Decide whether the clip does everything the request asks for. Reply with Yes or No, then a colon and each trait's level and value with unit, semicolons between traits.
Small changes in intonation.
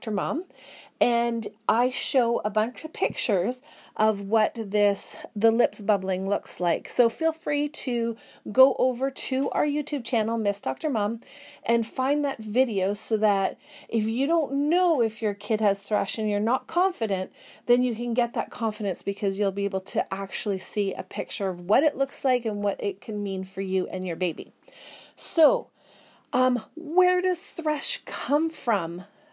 No: average, 5.1 semitones